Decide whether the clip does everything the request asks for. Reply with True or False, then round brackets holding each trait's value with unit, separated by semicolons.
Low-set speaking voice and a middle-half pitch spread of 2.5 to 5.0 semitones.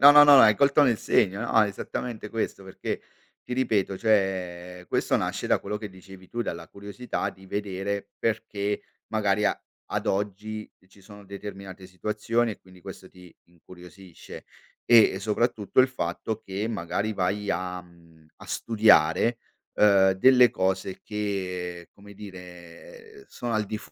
True (100 Hz; 2.8 semitones)